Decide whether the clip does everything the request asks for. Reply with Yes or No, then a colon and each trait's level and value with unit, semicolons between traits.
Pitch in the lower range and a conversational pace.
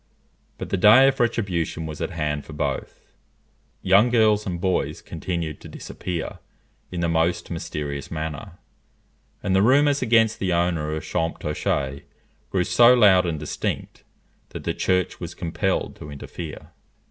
Yes: very low, 90 Hz; average, 145 wpm